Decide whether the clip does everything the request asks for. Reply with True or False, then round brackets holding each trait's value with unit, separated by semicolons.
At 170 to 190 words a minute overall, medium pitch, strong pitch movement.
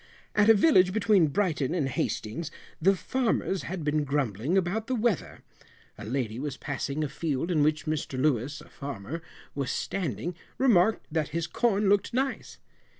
False (160 wpm; 160 Hz; 5.7 semitones)